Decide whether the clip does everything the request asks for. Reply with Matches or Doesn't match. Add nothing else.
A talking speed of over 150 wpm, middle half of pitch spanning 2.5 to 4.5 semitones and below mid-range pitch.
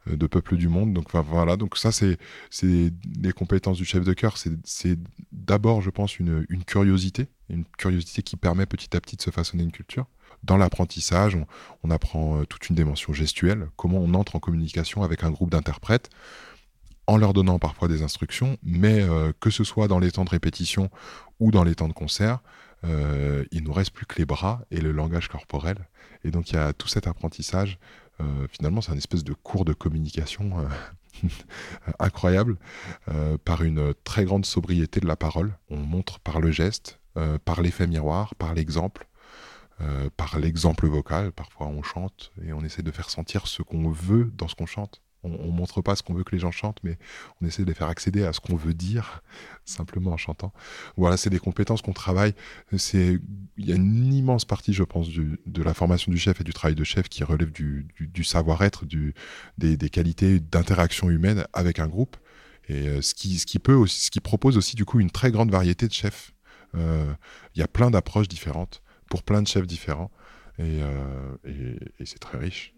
Matches